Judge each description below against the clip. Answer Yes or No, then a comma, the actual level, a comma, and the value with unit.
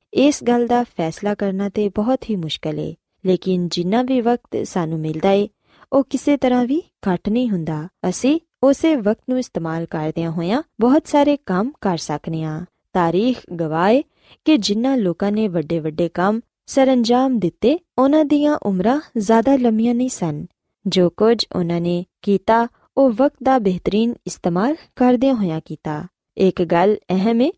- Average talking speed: Yes, average, 155 wpm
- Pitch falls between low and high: No, high, 215 Hz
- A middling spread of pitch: No, wide, 6.4 semitones